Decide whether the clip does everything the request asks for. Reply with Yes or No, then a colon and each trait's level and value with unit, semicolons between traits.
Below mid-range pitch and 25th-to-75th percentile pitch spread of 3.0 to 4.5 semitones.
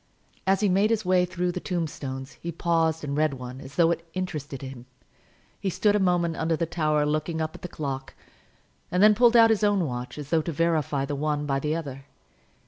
No: medium, 160 Hz; average, 4.0 semitones